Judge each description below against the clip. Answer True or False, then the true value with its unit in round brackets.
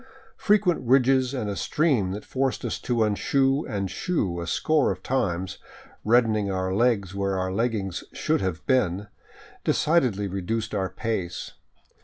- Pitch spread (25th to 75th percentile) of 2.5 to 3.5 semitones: False (5.4 semitones)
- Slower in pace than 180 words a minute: True (145 wpm)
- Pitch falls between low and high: False (110 Hz)